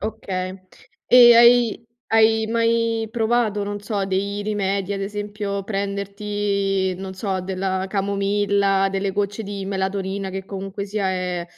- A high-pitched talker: Yes, high, 200 Hz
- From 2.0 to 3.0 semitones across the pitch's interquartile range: No, narrow, 1.5 semitones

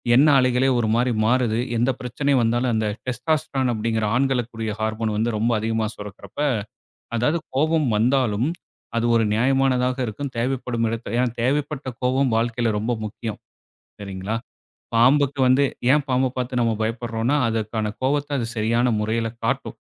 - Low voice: Yes, low, 120 Hz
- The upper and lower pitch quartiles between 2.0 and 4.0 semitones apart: Yes, average, 2.8 semitones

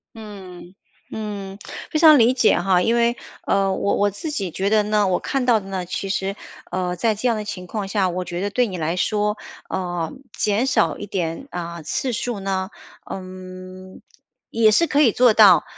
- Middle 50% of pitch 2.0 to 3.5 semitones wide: Yes, average, 3.1 semitones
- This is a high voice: Yes, high, 195 Hz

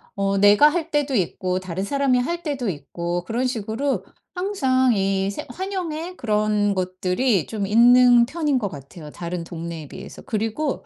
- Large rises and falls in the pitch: Yes, wide, 6.8 semitones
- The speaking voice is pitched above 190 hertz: Yes, high, 220 Hz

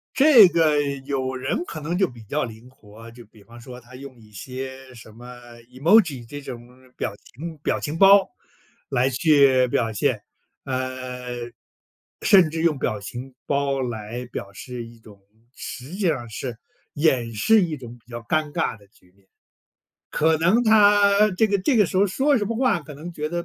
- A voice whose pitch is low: Yes, low, 130 Hz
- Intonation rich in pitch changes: Yes, wide, 5.9 semitones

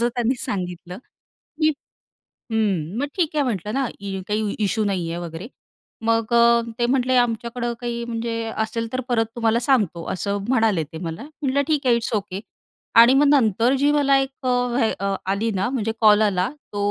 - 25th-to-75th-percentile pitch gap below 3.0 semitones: No, average, 3.8 semitones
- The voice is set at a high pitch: Yes, high, 230 Hz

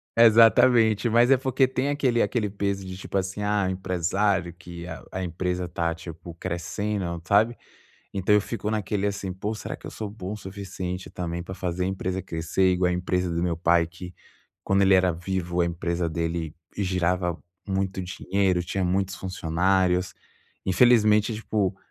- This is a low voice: Yes, very low, 95 Hz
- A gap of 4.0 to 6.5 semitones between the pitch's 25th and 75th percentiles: No, narrow, 2.6 semitones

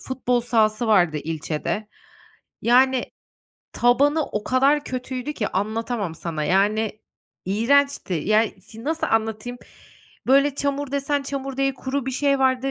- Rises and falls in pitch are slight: No, average, 4.3 semitones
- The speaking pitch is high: Yes, high, 245 Hz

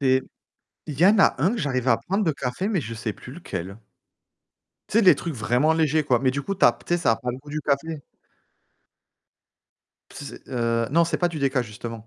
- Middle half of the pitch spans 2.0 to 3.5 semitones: No, average, 5.2 semitones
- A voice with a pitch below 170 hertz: Yes, medium, 140 Hz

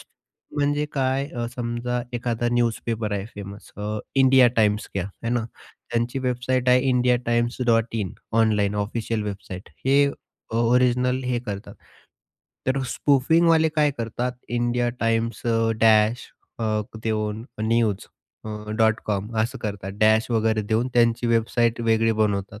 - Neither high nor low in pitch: No, low, 115 Hz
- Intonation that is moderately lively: No, narrow, 2.3 semitones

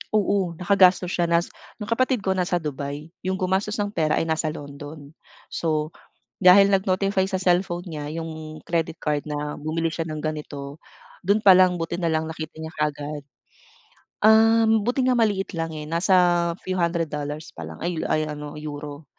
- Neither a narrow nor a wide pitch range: Yes, average, 3.7 semitones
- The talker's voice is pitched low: No, medium, 165 Hz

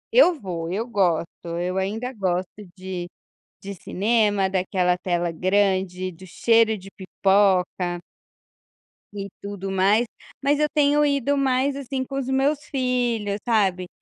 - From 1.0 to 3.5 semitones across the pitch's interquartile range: No, average, 5.3 semitones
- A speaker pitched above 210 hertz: No, high, 200 Hz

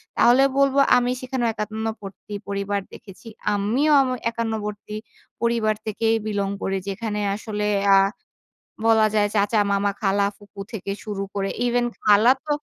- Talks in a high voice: Yes, high, 215 Hz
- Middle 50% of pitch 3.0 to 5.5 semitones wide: No, narrow, 2.4 semitones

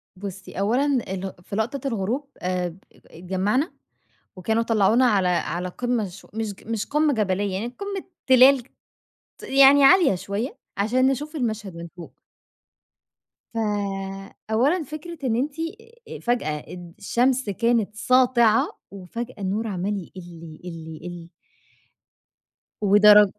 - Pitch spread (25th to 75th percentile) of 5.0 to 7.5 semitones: Yes, wide, 5.4 semitones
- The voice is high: Yes, high, 215 Hz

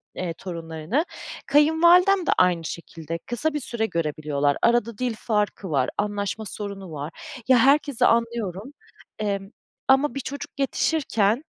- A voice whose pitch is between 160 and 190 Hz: No, high, 215 Hz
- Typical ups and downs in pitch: No, wide, 7.6 semitones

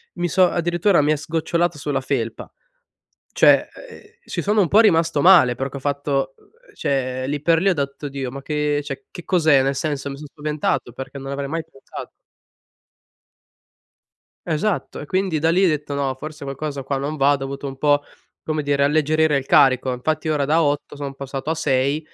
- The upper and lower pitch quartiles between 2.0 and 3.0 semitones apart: Yes, narrow, 2.5 semitones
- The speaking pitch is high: No, medium, 145 Hz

